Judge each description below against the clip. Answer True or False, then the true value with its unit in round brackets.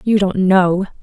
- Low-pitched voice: False (190 Hz)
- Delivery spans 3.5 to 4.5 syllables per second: True (3.9 syllables/s)